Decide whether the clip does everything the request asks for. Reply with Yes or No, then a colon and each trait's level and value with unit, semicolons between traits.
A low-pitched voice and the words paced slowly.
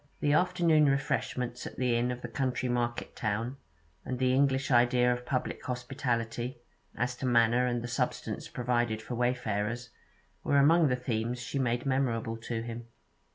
No: low, 125 Hz; average, 160 wpm